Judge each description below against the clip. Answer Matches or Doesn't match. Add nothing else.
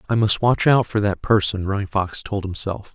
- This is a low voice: Matches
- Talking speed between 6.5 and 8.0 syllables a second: Doesn't match